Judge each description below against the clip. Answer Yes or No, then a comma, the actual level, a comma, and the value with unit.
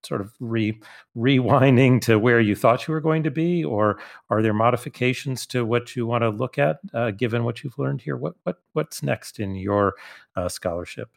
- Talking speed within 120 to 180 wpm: No, fast, 205 wpm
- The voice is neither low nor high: No, low, 120 Hz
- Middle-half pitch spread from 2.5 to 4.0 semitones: Yes, average, 3.3 semitones